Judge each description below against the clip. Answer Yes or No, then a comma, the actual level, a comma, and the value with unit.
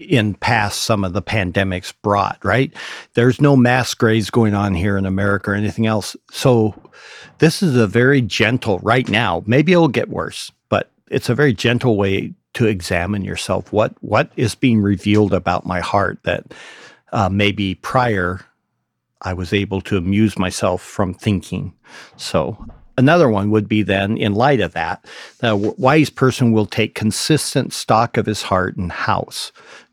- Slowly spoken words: No, average, 170 wpm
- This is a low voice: Yes, low, 105 Hz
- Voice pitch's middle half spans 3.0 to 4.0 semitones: Yes, average, 3.4 semitones